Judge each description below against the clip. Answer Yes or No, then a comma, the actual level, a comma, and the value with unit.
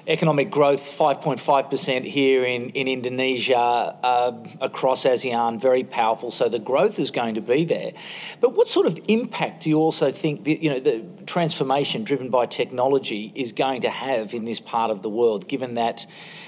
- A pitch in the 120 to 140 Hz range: Yes, low, 135 Hz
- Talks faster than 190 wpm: No, average, 180 wpm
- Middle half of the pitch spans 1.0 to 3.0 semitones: No, average, 4.4 semitones